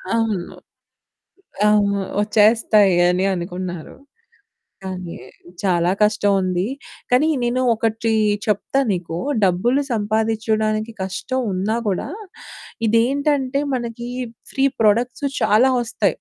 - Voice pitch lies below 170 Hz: No, high, 215 Hz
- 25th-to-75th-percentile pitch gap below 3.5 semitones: No, average, 4.1 semitones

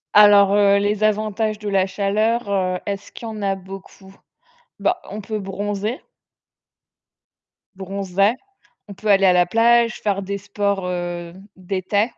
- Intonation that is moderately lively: No, narrow, 1.7 semitones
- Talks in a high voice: Yes, high, 200 Hz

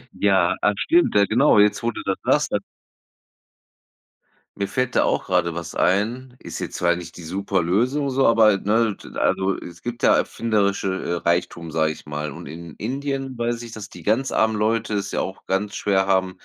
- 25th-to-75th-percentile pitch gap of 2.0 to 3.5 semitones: No, average, 4.7 semitones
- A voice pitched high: No, low, 100 Hz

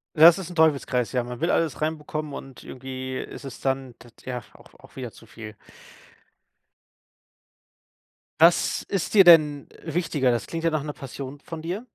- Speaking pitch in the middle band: Yes, medium, 145 Hz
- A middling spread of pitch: Yes, average, 4.1 semitones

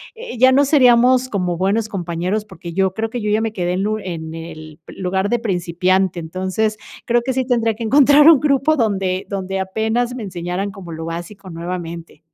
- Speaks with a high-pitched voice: Yes, high, 195 Hz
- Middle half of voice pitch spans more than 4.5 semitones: Yes, average, 4.9 semitones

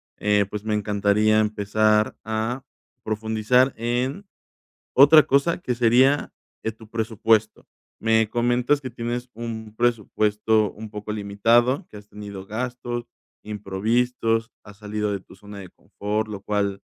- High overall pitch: No, low, 110 Hz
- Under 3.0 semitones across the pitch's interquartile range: Yes, narrow, 2.4 semitones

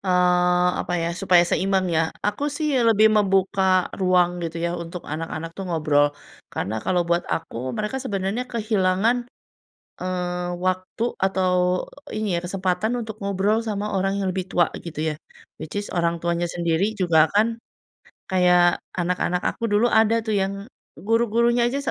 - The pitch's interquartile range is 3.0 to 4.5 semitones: Yes, average, 3.5 semitones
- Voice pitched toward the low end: No, medium, 185 Hz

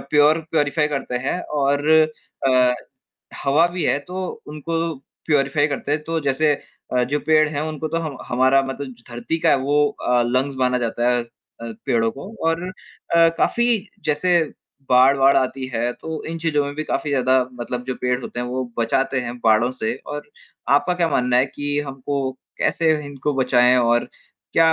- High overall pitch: No, medium, 140 Hz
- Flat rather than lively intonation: No, average, 3.5 semitones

